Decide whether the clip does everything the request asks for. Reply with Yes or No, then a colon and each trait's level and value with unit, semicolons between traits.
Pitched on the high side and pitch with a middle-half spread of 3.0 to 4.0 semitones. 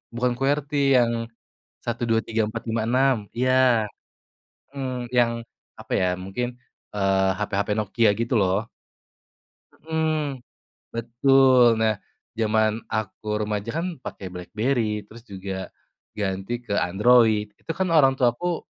No: low, 115 Hz; average, 3.6 semitones